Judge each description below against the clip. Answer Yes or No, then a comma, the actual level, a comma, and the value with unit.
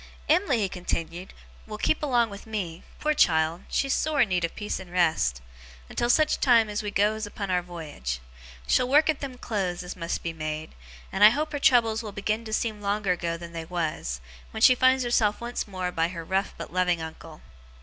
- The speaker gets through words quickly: Yes, fast, 210 wpm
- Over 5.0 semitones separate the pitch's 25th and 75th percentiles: Yes, wide, 5.6 semitones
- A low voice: No, high, 200 Hz